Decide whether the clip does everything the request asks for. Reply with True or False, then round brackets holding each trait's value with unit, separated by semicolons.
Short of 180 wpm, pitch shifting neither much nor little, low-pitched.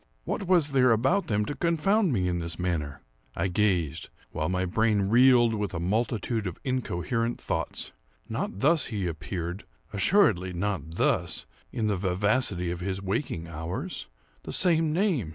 False (145 wpm; 6.3 semitones; 105 Hz)